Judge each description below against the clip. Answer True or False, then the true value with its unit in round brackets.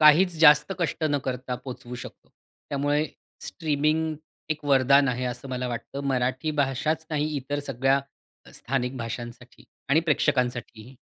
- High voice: False (135 Hz)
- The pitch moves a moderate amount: True (3.1 semitones)